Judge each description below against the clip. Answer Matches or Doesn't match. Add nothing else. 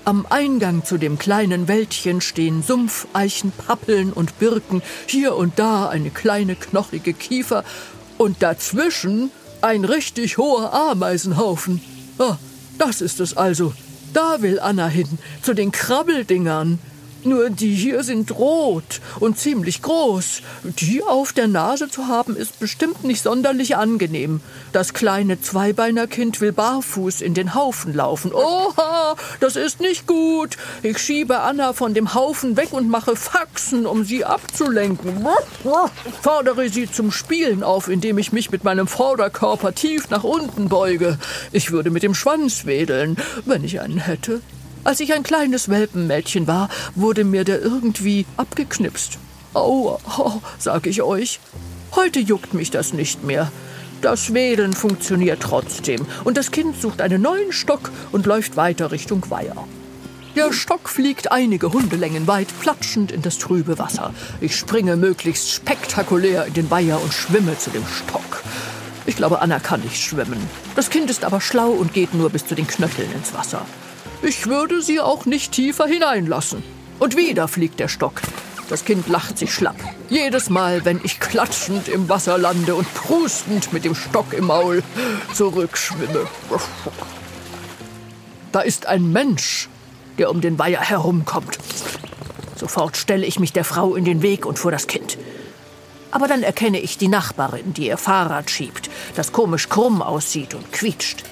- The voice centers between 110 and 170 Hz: Doesn't match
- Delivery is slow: Doesn't match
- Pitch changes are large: Matches